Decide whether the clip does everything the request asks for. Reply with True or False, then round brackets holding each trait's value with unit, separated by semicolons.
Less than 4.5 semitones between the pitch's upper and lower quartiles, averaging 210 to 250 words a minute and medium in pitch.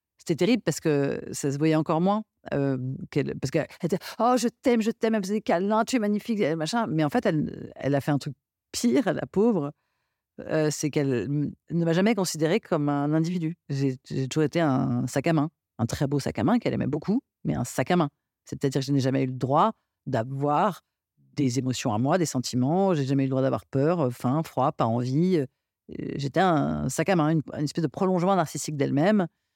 False (4.9 semitones; 220 wpm; 155 Hz)